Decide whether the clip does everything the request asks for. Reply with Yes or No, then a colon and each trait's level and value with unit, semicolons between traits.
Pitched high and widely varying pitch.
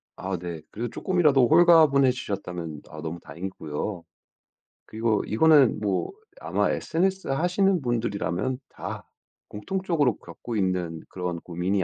No: low, 110 Hz; wide, 8.9 semitones